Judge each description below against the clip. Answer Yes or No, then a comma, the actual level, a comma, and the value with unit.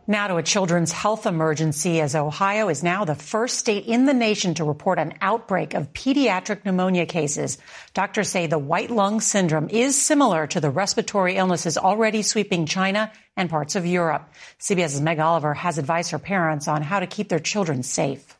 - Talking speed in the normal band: Yes, average, 185 wpm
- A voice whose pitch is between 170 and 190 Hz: Yes, medium, 185 Hz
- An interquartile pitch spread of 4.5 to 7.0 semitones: Yes, average, 4.8 semitones